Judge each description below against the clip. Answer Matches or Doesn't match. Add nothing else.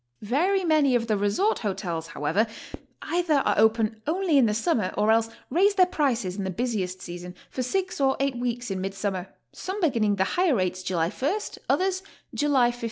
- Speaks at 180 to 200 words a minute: Matches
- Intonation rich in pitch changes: Matches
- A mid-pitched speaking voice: Doesn't match